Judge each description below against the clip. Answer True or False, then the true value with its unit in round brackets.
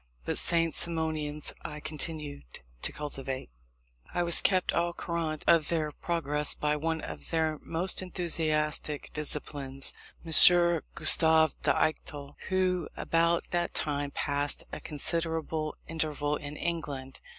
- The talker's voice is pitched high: False (155 Hz)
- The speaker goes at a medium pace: False (125 wpm)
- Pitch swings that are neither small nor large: False (2.2 semitones)